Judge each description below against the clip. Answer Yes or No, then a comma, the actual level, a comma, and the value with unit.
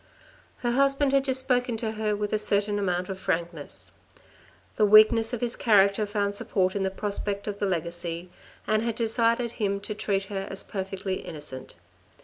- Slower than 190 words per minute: Yes, average, 175 wpm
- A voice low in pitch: No, high, 205 Hz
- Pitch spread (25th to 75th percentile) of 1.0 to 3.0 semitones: Yes, average, 2.7 semitones